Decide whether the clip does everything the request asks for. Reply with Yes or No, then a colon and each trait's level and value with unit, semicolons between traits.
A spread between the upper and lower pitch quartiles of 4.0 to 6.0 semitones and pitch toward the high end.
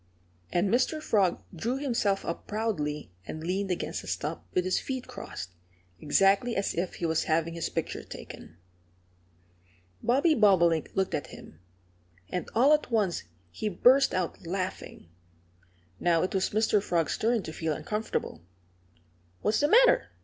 Yes: wide, 5.6 semitones; high, 195 Hz